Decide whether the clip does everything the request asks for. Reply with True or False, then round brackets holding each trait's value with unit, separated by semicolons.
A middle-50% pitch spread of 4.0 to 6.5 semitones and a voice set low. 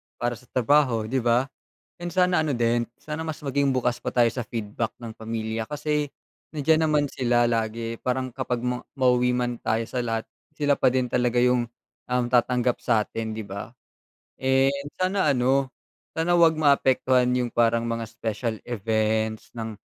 False (2.9 semitones; 125 Hz)